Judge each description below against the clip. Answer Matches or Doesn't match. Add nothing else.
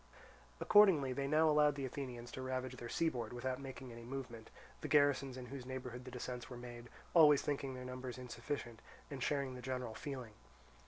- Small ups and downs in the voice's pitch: Matches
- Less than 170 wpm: Doesn't match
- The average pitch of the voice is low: Matches